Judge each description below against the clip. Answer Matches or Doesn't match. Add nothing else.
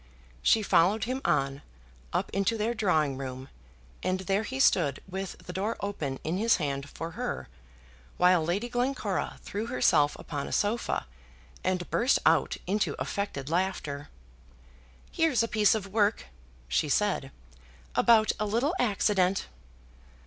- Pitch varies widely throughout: Matches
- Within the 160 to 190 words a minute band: Doesn't match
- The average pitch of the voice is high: Matches